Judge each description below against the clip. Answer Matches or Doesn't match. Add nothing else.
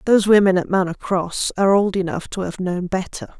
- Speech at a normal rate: Doesn't match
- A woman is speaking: Matches